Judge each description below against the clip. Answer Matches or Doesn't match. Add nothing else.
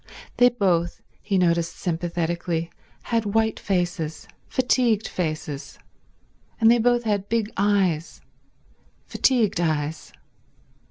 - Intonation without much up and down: Doesn't match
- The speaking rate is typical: Doesn't match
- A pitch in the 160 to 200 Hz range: Matches